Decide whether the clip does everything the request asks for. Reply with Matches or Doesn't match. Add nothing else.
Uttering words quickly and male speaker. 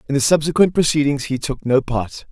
Matches